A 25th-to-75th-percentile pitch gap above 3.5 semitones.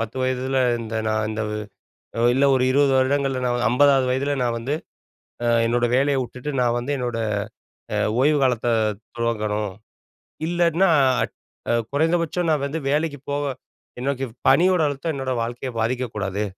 No: average, 3.2 semitones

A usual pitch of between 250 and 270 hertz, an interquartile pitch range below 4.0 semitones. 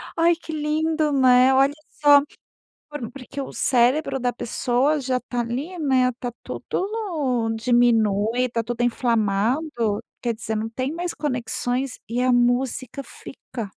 Yes: very high, 255 Hz; average, 3.3 semitones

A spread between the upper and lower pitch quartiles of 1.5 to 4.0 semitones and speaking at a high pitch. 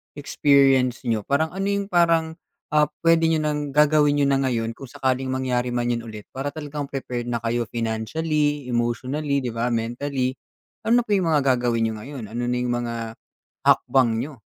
No: average, 3.7 semitones; low, 130 Hz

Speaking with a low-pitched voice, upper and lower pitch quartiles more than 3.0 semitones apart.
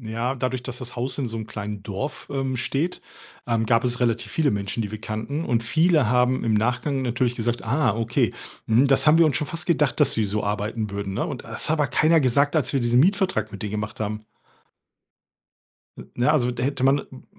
Yes: low, 120 Hz; average, 4.0 semitones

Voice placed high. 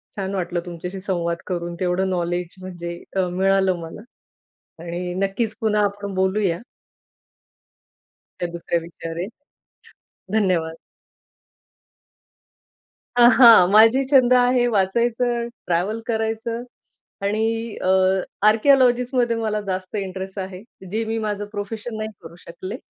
Yes: high, 195 Hz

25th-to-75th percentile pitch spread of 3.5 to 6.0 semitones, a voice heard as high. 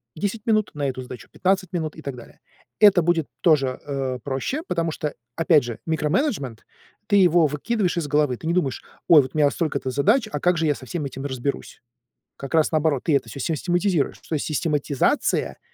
No: average, 4.1 semitones; medium, 155 Hz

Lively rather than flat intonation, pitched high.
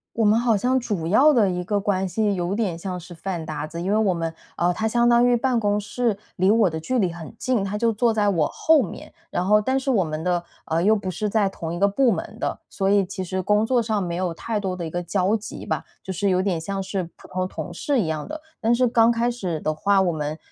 No: average, 4.2 semitones; high, 200 Hz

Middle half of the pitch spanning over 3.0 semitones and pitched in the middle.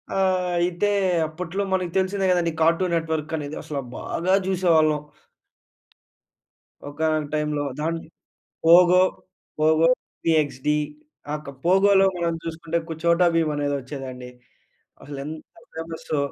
No: narrow, 2.6 semitones; medium, 160 Hz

